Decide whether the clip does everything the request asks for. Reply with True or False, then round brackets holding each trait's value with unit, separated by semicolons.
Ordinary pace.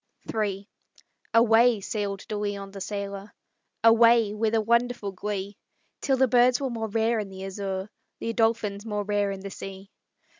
True (160 wpm)